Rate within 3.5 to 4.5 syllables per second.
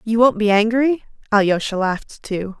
No: 5.0 syllables/s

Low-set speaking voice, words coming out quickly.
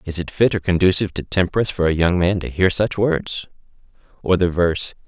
Yes: very low, 90 Hz; fast, 215 wpm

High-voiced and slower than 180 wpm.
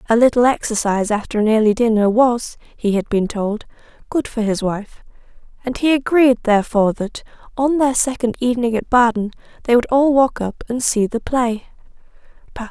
Yes: high, 230 Hz; average, 170 wpm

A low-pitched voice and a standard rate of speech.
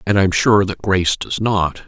No: very low, 95 Hz; fast, 255 wpm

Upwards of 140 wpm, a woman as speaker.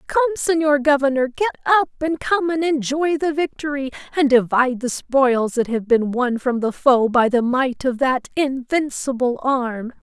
Yes: average, 170 wpm; female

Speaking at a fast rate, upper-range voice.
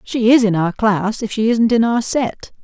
Yes: fast, 250 wpm; high, 220 Hz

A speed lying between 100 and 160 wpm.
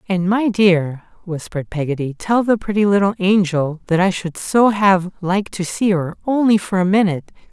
No: average, 185 wpm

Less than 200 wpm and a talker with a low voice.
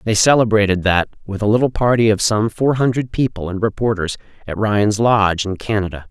Yes: average, 185 wpm; low, 105 Hz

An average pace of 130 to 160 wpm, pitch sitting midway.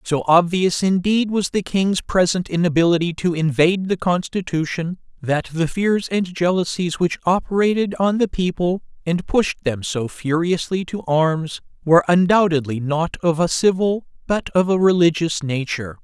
Yes: average, 150 wpm; medium, 175 Hz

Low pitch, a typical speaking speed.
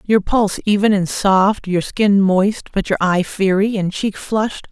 No: high, 200 Hz; average, 190 wpm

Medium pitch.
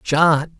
Yes: medium, 155 Hz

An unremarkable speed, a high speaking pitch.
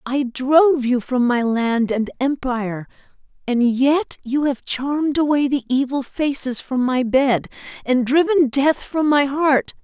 Yes: average, 160 wpm; very high, 265 Hz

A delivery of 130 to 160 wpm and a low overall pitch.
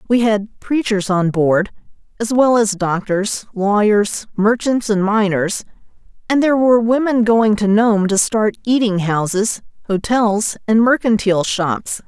No: average, 140 wpm; high, 215 Hz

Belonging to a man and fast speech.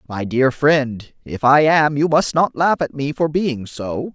Yes: male; fast, 215 wpm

